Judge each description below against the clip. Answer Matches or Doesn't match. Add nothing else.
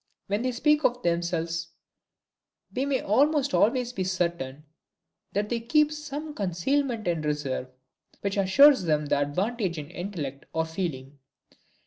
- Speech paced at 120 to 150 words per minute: Matches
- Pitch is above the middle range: Matches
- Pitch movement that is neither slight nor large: Doesn't match